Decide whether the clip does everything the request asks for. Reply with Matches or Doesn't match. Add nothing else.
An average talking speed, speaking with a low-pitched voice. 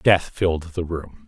Matches